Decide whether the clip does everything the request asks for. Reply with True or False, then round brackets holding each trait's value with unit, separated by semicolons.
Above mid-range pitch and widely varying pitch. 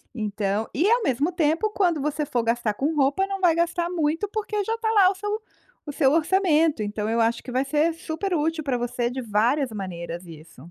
True (295 Hz; 7.1 semitones)